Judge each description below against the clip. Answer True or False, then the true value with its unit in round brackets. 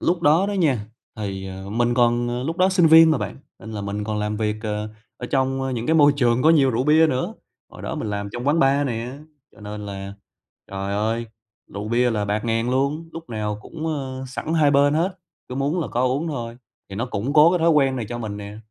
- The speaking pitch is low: True (125 Hz)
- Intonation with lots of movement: True (5.9 semitones)